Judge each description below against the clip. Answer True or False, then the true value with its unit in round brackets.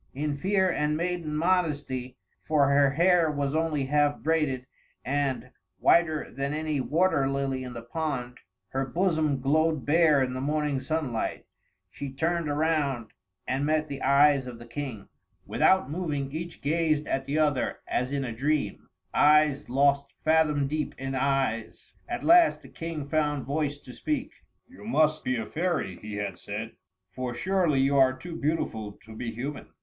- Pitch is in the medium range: True (145 Hz)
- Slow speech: False (165 wpm)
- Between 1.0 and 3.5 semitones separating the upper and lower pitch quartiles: True (3.0 semitones)